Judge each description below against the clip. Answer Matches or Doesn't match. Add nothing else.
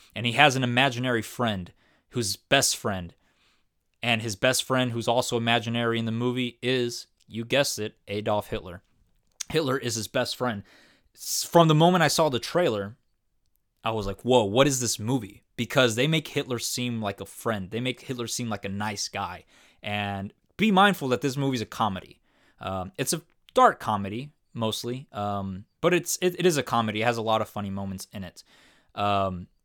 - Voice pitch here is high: Doesn't match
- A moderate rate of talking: Matches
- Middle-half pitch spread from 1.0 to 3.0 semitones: Doesn't match